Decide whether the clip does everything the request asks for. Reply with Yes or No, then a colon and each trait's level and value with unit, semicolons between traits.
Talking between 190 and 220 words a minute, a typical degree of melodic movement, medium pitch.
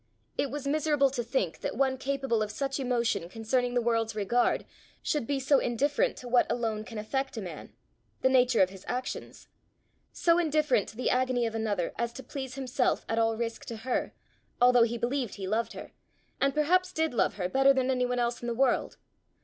No: fast, 205 wpm; average, 3.1 semitones; high, 245 Hz